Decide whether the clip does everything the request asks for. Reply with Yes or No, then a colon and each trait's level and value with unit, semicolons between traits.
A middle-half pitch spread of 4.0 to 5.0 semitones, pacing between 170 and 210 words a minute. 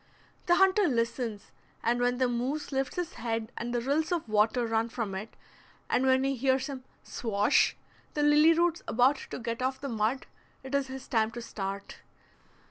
No: average, 3.3 semitones; average, 180 wpm